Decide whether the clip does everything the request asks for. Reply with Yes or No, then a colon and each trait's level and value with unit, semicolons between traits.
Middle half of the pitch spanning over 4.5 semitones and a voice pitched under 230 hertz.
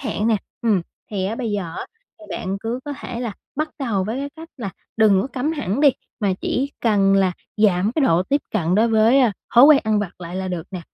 Yes: average, 5.1 semitones; high, 215 Hz